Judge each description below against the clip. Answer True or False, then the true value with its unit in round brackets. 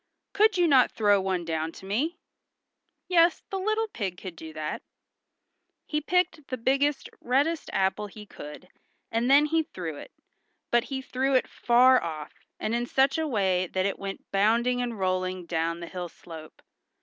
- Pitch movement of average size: False (7.1 semitones)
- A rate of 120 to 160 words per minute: False (175 wpm)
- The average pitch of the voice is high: True (230 Hz)